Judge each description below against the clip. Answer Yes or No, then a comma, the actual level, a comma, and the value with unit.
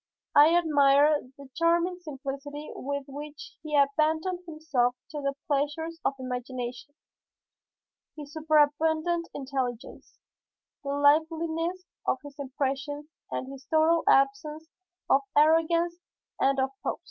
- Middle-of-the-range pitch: No, very high, 295 Hz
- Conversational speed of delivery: No, slow, 110 wpm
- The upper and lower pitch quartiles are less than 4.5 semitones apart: Yes, average, 2.7 semitones